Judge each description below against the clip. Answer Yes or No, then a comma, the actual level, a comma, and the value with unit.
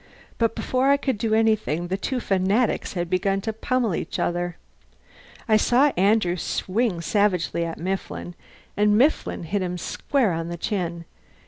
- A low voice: No, high, 195 Hz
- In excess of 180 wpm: No, average, 155 wpm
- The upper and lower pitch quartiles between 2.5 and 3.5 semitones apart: No, average, 4.3 semitones